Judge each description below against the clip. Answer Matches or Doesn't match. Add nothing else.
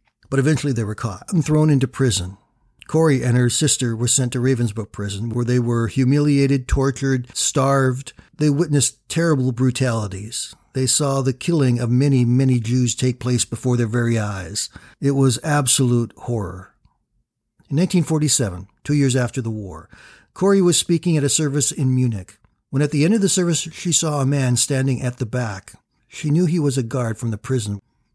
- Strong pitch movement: Doesn't match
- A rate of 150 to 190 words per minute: Matches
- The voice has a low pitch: Matches